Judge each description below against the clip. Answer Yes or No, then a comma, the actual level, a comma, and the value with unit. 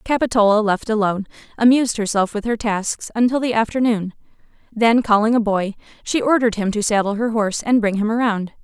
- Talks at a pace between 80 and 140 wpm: No, average, 180 wpm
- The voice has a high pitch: Yes, high, 220 Hz